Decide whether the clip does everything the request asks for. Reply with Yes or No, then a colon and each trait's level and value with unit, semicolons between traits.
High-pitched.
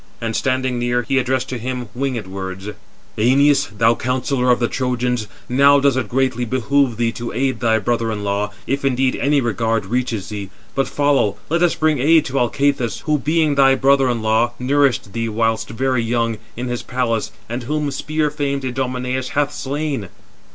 No: low, 125 Hz